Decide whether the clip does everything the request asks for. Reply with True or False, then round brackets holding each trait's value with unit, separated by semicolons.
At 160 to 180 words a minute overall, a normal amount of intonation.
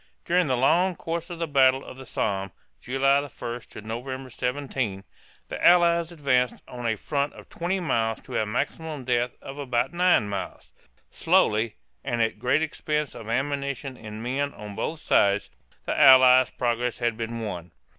True (165 wpm; 4.1 semitones)